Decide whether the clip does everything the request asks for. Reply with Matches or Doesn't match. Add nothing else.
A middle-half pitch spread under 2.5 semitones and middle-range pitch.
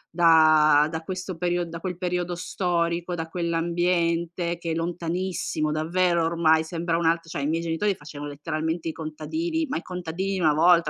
Matches